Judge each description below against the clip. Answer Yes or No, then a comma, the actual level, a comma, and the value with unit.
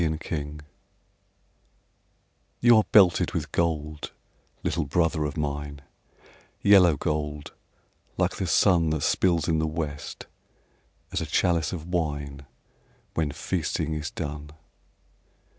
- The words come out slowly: Yes, slow, 120 wpm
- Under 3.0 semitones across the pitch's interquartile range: Yes, narrow, 2.5 semitones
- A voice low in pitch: Yes, very low, 80 Hz